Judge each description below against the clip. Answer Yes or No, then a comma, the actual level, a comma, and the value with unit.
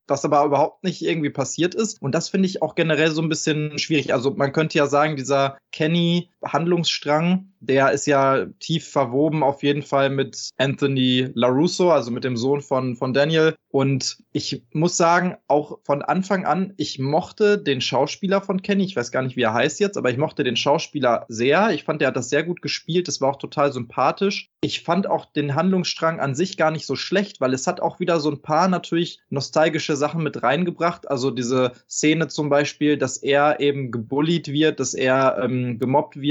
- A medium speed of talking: No, fast, 205 wpm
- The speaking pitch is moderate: Yes, medium, 150 Hz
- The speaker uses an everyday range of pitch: Yes, average, 3.6 semitones